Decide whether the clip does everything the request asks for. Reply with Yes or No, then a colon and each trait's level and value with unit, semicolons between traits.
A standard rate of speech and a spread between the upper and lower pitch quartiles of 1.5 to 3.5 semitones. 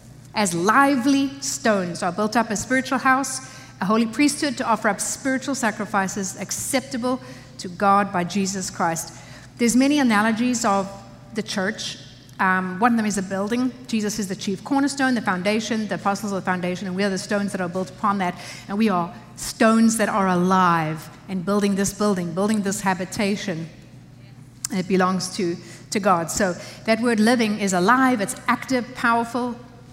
No: average, 175 wpm; average, 3.9 semitones